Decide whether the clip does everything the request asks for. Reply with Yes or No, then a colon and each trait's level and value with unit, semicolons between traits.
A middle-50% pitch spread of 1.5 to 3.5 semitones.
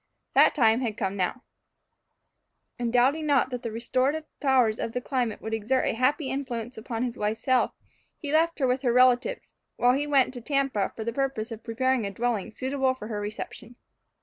Yes: average, 2.9 semitones